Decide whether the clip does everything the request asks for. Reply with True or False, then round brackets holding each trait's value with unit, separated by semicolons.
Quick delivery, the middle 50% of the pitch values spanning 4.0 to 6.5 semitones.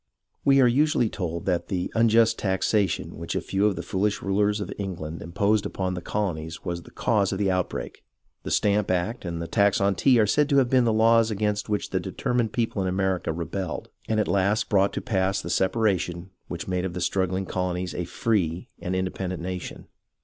False (210 wpm; 3.1 semitones)